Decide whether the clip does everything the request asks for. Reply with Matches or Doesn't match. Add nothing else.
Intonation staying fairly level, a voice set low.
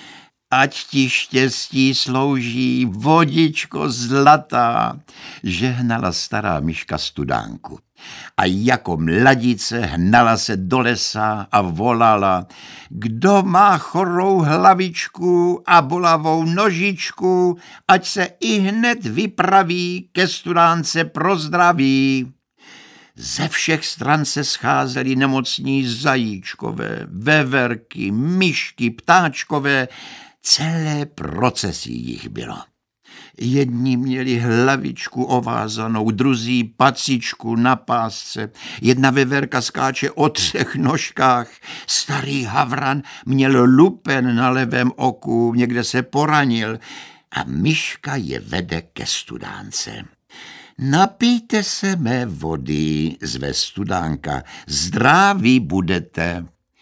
Doesn't match